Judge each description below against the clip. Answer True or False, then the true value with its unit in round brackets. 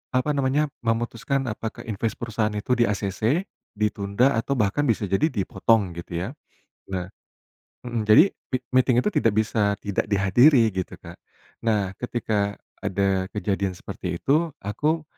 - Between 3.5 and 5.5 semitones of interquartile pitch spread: True (4.1 semitones)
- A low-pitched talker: True (110 Hz)